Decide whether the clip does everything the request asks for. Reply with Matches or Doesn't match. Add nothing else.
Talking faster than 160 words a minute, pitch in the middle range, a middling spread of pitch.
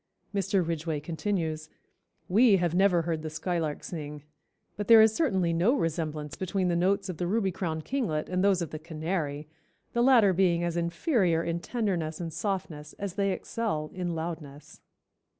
Matches